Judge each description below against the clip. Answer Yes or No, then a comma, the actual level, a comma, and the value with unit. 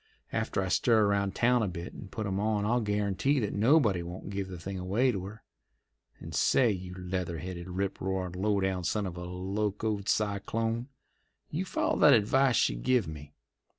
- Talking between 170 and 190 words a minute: Yes, average, 185 wpm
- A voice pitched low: Yes, low, 100 Hz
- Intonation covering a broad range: No, average, 2.9 semitones